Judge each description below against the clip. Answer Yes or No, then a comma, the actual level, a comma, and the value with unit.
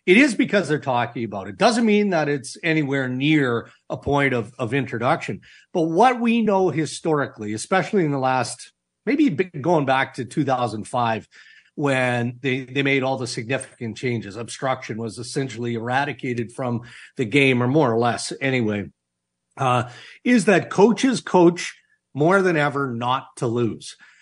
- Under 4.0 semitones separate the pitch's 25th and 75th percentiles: No, average, 4.9 semitones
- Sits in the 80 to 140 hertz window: Yes, low, 135 Hz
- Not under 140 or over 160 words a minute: Yes, average, 155 wpm